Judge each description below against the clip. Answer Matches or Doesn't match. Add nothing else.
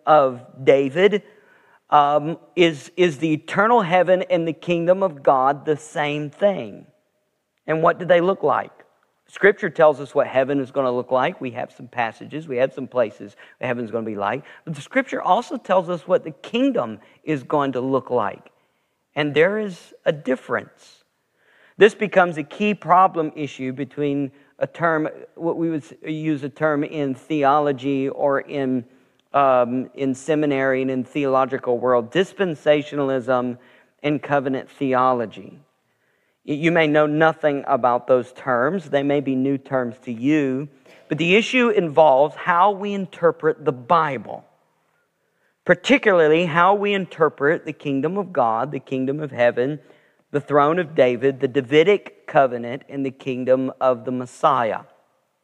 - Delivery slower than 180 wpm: Matches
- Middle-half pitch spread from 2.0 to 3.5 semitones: Doesn't match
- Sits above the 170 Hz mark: Doesn't match